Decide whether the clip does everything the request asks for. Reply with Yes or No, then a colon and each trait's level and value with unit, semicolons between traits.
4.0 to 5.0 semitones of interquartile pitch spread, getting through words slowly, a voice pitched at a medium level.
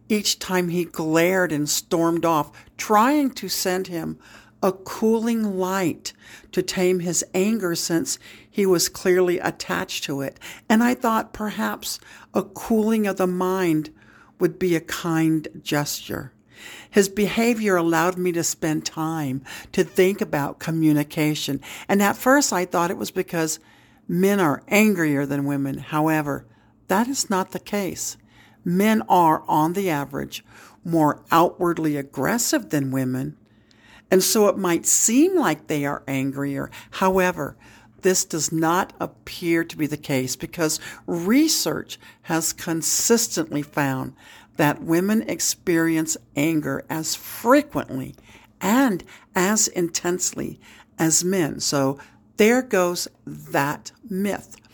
Yes: average, 4.6 semitones; slow, 130 wpm; medium, 170 Hz